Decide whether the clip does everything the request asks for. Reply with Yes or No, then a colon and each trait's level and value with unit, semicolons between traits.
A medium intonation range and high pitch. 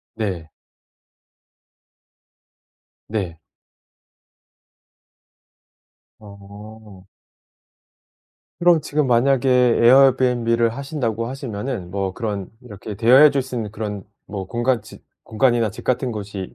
No: average, 3.9 semitones; low, 115 Hz